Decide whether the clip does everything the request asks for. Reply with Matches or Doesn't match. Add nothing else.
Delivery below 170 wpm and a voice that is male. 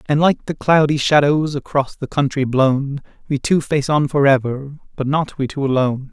Doesn't match